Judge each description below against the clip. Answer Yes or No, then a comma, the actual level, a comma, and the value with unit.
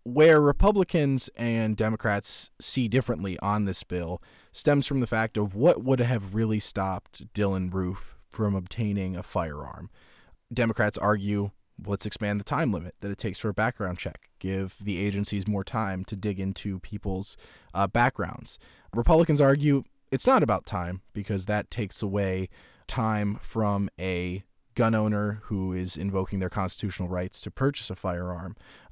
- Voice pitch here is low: Yes, low, 105 Hz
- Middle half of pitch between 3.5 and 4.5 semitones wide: No, average, 3.0 semitones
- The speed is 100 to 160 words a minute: Yes, average, 155 wpm